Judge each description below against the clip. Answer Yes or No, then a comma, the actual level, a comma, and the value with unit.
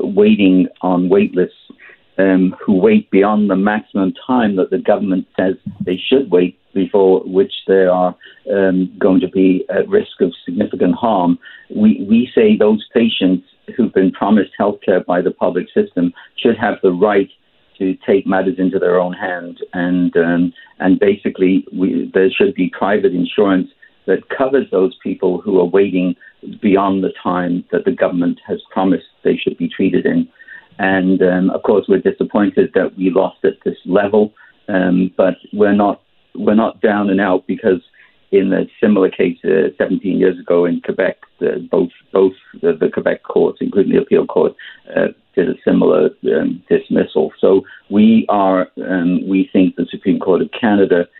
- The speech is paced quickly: No, average, 170 wpm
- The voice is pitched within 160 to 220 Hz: No, very low, 95 Hz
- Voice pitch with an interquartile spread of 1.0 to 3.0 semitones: Yes, narrow, 2.5 semitones